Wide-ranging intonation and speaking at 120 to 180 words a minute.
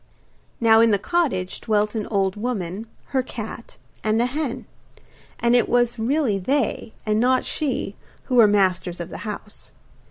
No: average, 3.2 semitones; average, 160 wpm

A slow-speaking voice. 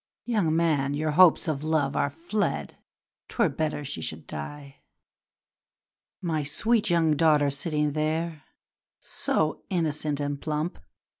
Yes: slow, 125 wpm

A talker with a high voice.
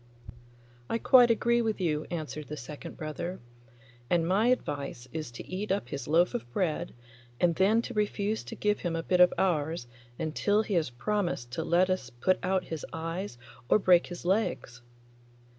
No: medium, 175 Hz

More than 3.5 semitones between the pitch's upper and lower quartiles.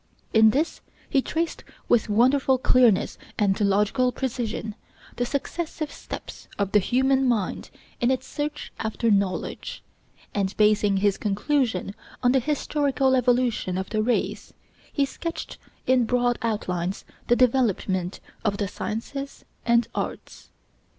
Yes: average, 4.2 semitones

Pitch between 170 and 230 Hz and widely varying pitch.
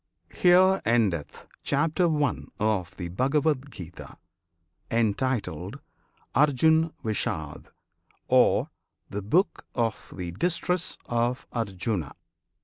No: low, 120 Hz; wide, 7.9 semitones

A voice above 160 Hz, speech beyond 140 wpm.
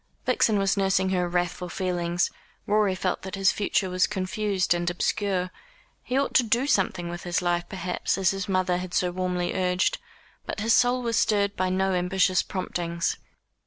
Yes: medium, 185 Hz; average, 175 wpm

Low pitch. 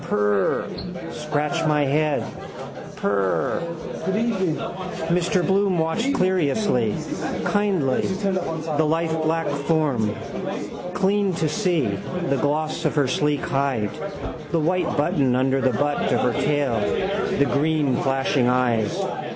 No: medium, 150 Hz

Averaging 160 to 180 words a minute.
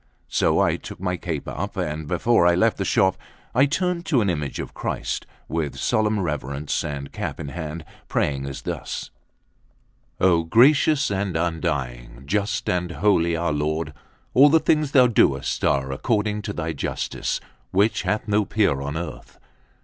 Yes: average, 165 wpm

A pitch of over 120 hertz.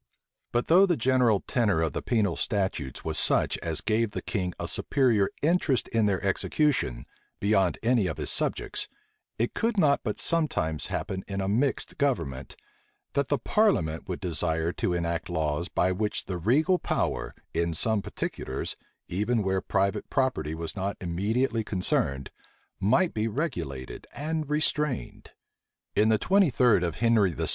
No: low, 105 Hz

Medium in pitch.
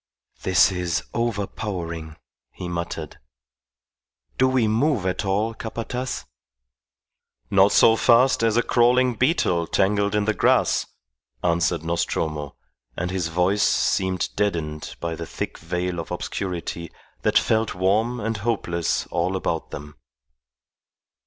No: very low, 95 Hz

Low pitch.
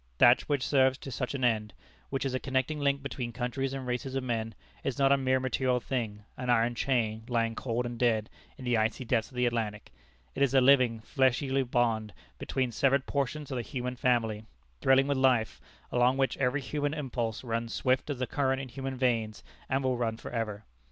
Yes: low, 125 Hz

